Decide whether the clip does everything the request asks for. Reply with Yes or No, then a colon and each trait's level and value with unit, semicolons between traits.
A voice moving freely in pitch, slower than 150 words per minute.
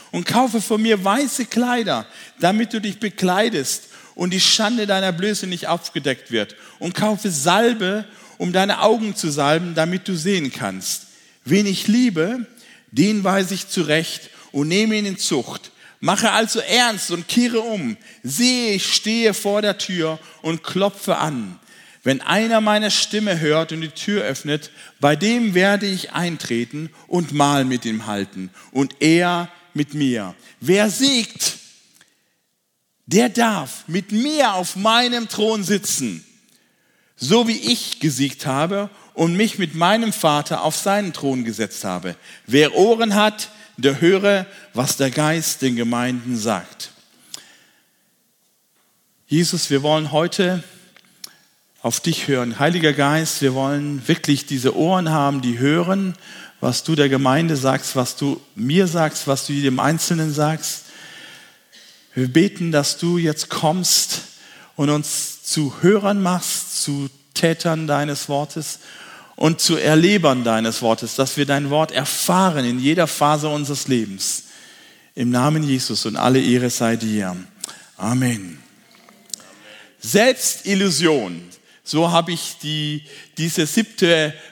Yes: wide, 6.1 semitones; average, 140 wpm